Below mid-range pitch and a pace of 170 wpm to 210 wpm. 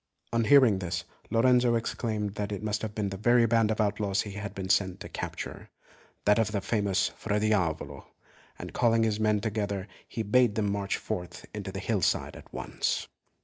Yes: low, 105 Hz; average, 190 wpm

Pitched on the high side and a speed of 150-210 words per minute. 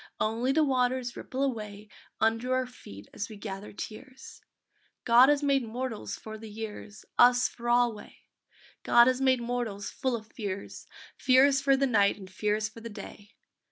Yes: high, 235 Hz; average, 165 wpm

